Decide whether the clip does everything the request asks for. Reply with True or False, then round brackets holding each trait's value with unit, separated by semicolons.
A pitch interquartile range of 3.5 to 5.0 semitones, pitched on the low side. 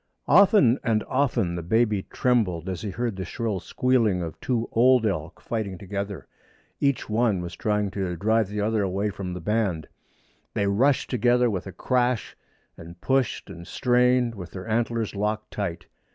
True (4.2 semitones; 105 Hz)